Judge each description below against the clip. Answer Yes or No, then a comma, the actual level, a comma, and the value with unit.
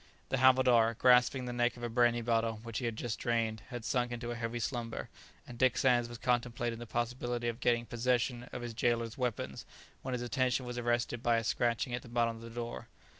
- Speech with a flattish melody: Yes, narrow, 0.9 semitones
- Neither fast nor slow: No, fast, 220 wpm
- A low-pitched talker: Yes, low, 120 Hz